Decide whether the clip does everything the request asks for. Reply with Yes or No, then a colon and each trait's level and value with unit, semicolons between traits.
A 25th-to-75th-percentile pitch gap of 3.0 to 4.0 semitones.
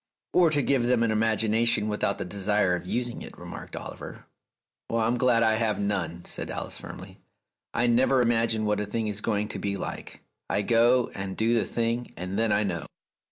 No: narrow, 2.5 semitones